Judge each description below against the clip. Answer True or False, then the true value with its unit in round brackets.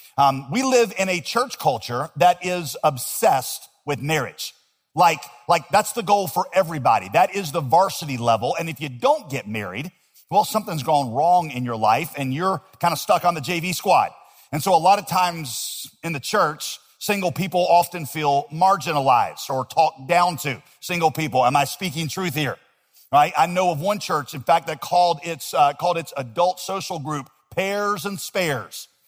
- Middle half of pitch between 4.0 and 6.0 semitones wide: True (4.4 semitones)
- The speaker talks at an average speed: True (190 wpm)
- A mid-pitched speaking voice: True (170 Hz)